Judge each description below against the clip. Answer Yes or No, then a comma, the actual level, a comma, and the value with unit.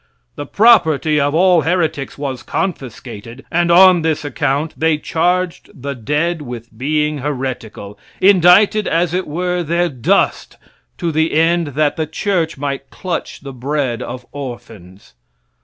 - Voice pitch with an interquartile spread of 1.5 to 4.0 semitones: No, average, 4.4 semitones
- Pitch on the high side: No, medium, 150 Hz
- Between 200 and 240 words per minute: No, average, 140 wpm